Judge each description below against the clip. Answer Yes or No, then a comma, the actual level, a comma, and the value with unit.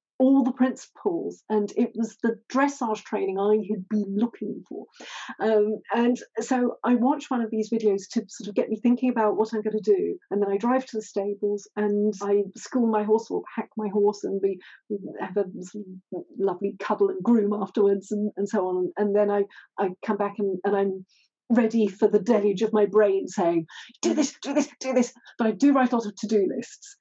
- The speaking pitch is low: No, high, 215 Hz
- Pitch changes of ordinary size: Yes, average, 3.1 semitones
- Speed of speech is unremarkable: No, fast, 215 wpm